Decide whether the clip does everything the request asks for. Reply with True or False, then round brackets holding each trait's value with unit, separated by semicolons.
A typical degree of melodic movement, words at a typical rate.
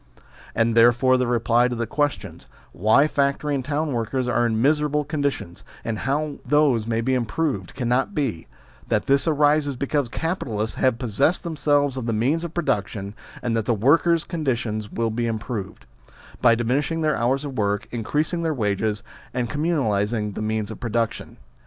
True (4.5 semitones; 175 wpm)